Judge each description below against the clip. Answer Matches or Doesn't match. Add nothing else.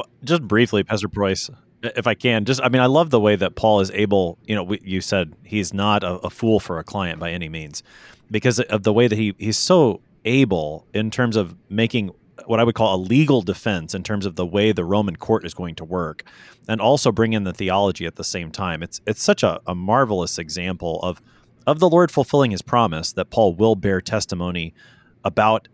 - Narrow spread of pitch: Doesn't match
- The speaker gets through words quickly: Matches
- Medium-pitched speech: Doesn't match